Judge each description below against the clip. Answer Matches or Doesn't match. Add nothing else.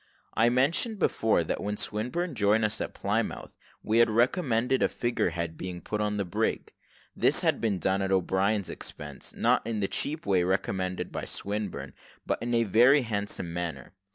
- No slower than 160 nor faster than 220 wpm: Matches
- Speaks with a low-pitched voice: Matches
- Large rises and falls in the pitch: Doesn't match